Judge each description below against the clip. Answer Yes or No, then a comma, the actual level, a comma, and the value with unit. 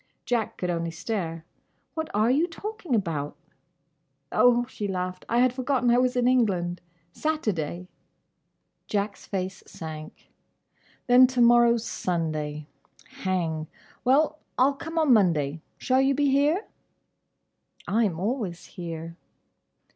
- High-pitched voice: Yes, high, 215 Hz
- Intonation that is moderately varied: No, wide, 6.9 semitones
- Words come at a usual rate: No, slow, 125 wpm